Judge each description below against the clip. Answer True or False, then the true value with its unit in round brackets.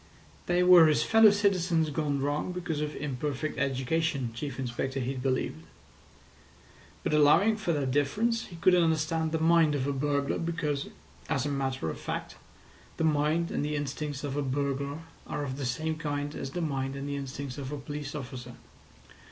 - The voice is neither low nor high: True (145 Hz)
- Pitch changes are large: False (2.9 semitones)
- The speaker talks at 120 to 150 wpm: False (175 wpm)